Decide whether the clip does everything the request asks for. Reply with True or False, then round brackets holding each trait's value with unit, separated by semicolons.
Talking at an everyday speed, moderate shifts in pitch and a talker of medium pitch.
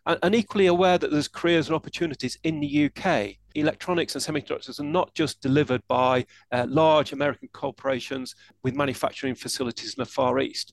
True (170 wpm; 3.6 semitones; 145 Hz)